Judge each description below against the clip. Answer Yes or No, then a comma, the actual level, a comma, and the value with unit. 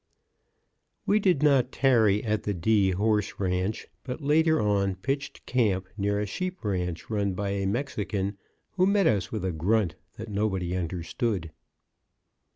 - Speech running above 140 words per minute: Yes, average, 155 wpm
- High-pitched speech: No, low, 105 Hz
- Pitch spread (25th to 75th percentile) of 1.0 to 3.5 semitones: No, average, 4.9 semitones